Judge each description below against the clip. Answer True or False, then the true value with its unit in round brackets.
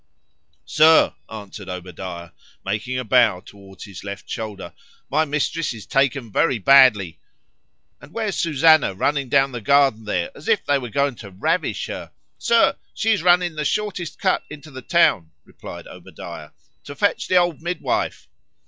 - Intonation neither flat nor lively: False (8.1 semitones)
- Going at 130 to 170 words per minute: True (150 wpm)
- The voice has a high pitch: False (135 Hz)